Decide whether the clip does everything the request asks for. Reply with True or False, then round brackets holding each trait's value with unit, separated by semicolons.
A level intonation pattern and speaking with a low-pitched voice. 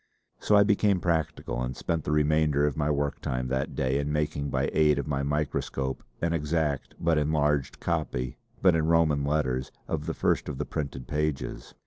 True (2.2 semitones; 75 Hz)